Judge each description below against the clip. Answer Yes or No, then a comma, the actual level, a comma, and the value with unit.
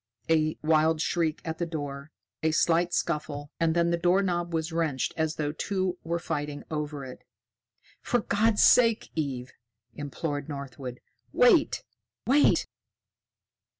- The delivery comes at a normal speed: No, slow, 130 wpm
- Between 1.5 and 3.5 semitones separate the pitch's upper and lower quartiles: Yes, average, 2.9 semitones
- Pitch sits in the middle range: Yes, medium, 160 Hz